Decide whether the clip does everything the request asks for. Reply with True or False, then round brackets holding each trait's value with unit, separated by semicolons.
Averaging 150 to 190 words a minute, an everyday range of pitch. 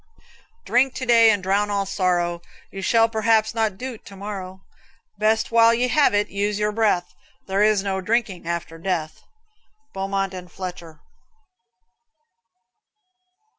False (135 wpm; 3.1 semitones)